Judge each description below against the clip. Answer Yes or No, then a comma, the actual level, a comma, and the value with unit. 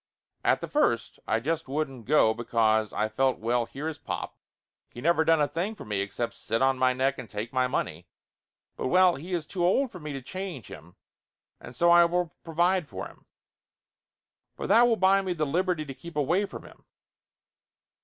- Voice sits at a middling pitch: Yes, medium, 145 Hz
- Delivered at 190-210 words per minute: Yes, average, 200 wpm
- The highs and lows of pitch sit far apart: Yes, wide, 6.5 semitones